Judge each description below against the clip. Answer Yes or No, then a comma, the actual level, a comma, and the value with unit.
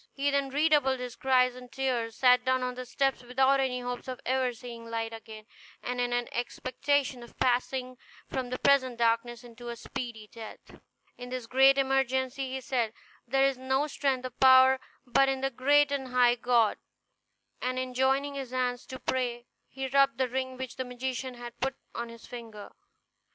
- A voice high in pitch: Yes, very high, 255 Hz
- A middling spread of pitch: No, narrow, 1.6 semitones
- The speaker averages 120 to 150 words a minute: No, average, 185 wpm